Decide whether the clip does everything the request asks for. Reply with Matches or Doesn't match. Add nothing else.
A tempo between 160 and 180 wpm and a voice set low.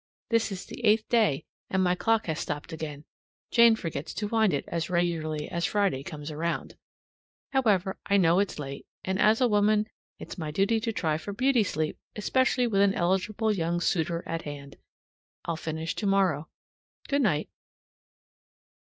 Doesn't match